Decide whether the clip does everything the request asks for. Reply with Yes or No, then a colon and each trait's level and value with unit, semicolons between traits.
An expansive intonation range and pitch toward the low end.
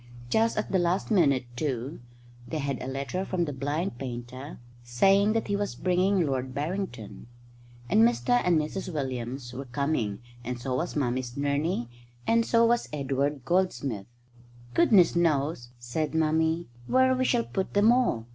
No: wide, 6.7 semitones; medium, 155 Hz